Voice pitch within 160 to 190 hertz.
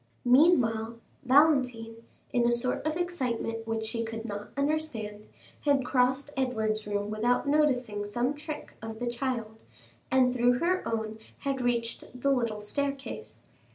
No: high, 245 Hz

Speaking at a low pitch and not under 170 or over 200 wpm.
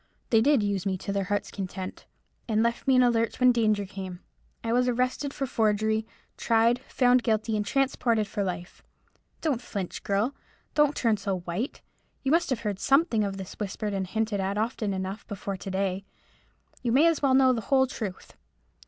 No: high, 220 Hz; average, 190 wpm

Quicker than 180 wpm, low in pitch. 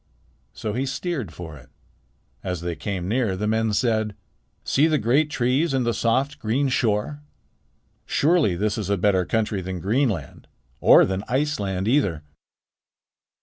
No: average, 145 wpm; low, 110 Hz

